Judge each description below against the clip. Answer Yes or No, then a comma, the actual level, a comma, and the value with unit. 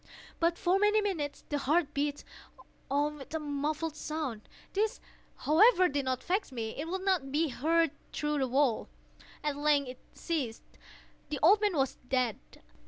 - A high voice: Yes, very high, 300 Hz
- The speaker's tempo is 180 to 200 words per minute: No, average, 165 wpm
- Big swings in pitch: No, average, 3.6 semitones